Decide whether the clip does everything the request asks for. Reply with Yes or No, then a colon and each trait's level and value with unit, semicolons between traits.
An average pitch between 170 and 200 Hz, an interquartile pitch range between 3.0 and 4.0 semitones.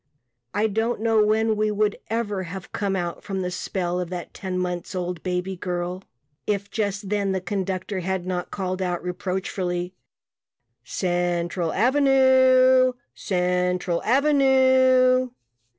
Yes: high, 190 Hz; average, 3.7 semitones